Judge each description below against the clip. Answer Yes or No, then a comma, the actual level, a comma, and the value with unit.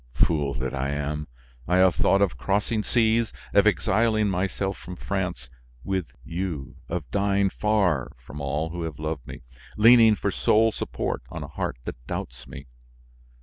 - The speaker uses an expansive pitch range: Yes, wide, 5.7 semitones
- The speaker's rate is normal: Yes, average, 160 wpm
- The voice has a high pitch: No, very low, 90 Hz